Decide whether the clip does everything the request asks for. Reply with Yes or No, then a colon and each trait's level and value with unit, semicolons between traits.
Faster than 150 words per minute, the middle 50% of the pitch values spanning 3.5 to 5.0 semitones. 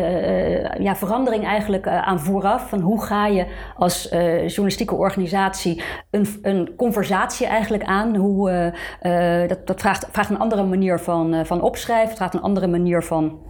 No: average, 175 wpm; average, 2.9 semitones